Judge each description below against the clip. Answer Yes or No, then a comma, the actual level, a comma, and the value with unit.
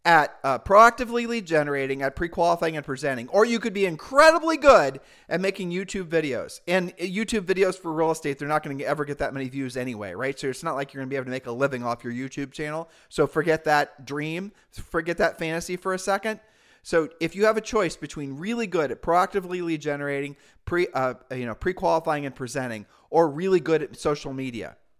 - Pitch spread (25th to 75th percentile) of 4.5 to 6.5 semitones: Yes, average, 5.1 semitones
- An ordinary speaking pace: No, fast, 210 wpm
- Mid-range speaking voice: Yes, medium, 160 Hz